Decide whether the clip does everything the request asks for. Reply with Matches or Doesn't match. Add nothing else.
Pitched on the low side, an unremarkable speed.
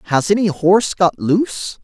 Doesn't match